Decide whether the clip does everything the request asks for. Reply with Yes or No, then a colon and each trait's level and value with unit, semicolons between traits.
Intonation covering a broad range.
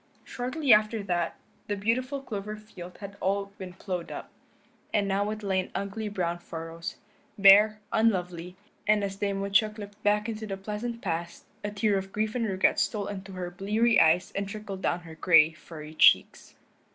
No: average, 2.7 semitones